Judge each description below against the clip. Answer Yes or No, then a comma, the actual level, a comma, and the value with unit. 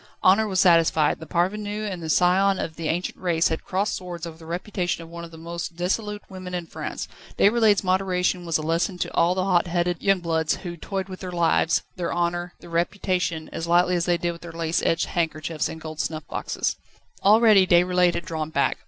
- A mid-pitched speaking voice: Yes, medium, 175 Hz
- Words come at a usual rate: No, fast, 215 wpm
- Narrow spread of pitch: Yes, narrow, 1.9 semitones